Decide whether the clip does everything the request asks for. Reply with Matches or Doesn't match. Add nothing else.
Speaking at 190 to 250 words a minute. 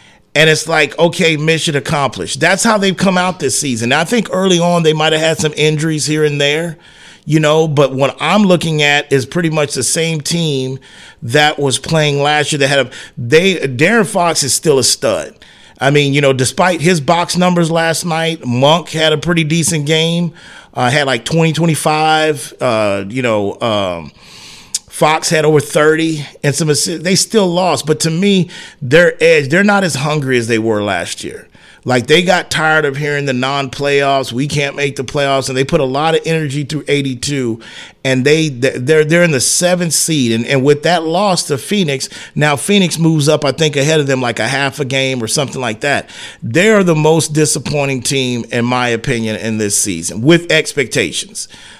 Matches